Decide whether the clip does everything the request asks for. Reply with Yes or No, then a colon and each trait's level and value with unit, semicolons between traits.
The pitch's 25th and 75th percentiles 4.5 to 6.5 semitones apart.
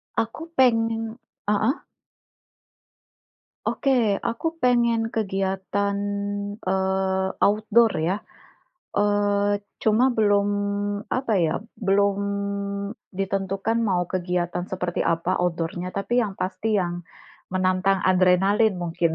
No: average, 3.2 semitones